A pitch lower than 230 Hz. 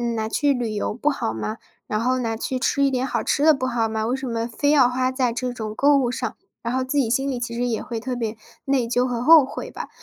No: very high, 250 Hz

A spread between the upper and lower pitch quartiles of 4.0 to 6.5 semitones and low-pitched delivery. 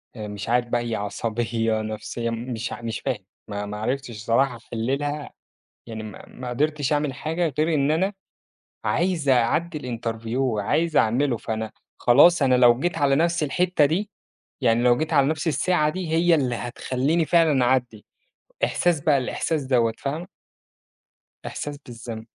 Yes: average, 4.9 semitones; low, 130 Hz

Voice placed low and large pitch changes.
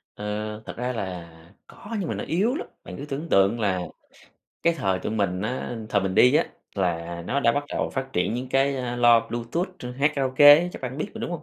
Yes: low, 125 Hz; wide, 6.3 semitones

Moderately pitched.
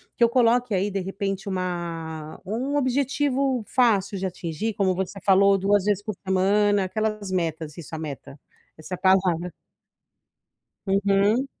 No: high, 195 Hz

